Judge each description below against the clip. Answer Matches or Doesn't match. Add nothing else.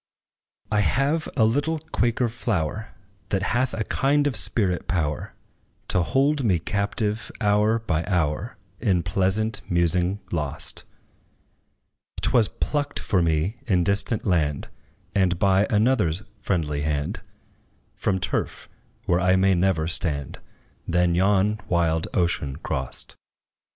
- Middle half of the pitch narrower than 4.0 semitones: Doesn't match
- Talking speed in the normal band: Doesn't match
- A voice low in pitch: Matches